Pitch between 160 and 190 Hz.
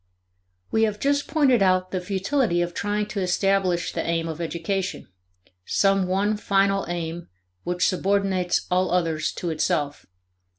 Yes: medium, 185 Hz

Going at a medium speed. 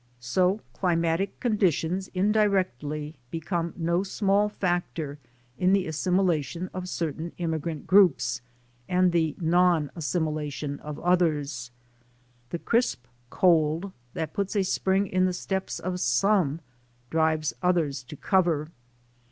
No: slow, 115 wpm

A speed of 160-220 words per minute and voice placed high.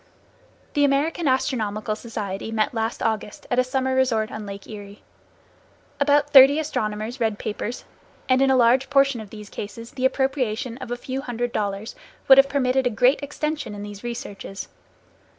Yes: average, 170 wpm; high, 245 Hz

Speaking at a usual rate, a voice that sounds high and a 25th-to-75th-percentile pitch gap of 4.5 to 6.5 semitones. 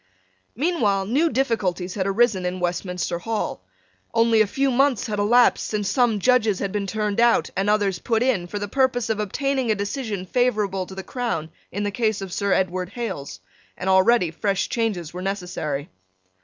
No: average, 180 wpm; high, 205 Hz; average, 4.0 semitones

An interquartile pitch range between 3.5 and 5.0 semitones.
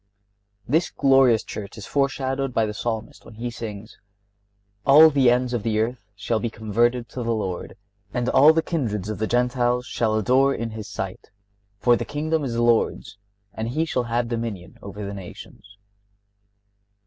No: average, 3.1 semitones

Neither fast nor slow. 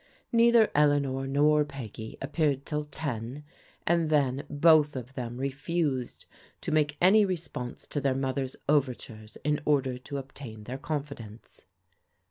No: slow, 130 wpm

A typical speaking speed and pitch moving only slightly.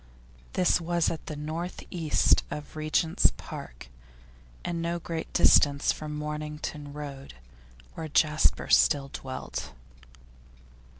No: slow, 110 wpm; narrow, 2.0 semitones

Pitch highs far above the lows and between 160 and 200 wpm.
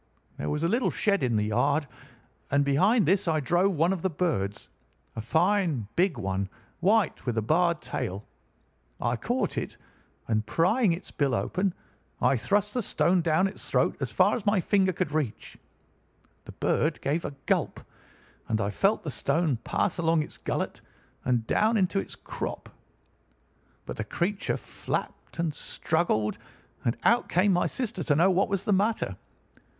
Yes: wide, 6.3 semitones; average, 165 wpm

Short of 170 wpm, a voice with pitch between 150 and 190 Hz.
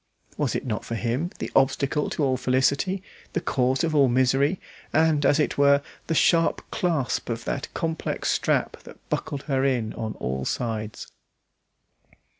No: average, 160 wpm; low, 135 Hz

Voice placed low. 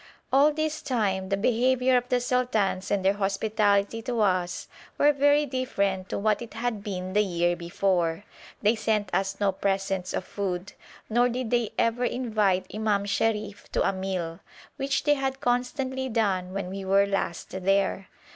No: high, 205 Hz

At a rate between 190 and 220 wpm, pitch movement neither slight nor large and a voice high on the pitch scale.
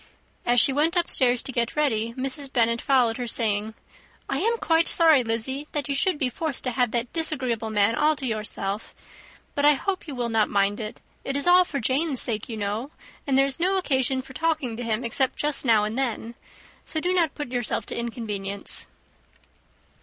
Yes: average, 200 wpm; average, 4.6 semitones; very high, 255 Hz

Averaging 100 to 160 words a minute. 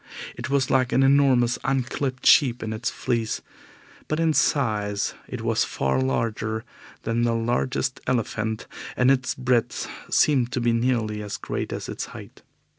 Yes: average, 155 wpm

